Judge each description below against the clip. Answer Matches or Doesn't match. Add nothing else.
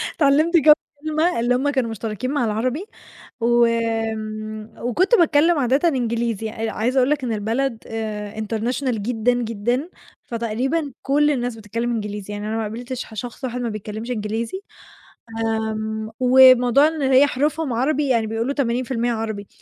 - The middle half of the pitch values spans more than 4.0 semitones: Doesn't match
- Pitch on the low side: Doesn't match